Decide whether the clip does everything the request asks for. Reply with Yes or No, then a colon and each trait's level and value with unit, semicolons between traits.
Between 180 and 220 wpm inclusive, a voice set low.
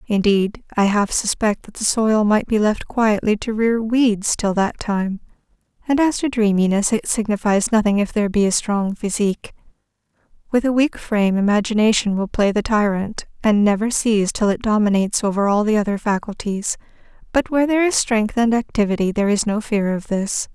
No: average, 185 wpm; high, 215 Hz